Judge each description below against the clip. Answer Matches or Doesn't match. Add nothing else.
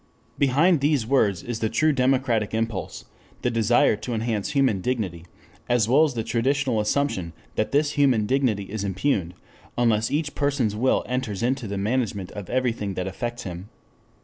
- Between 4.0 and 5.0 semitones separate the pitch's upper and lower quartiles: Matches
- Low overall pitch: Matches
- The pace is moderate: Matches